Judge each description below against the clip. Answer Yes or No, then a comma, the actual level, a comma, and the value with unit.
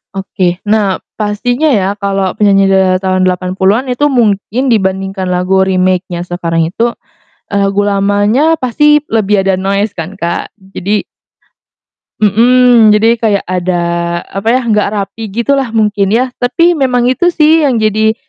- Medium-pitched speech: No, high, 205 Hz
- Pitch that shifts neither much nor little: Yes, average, 4.0 semitones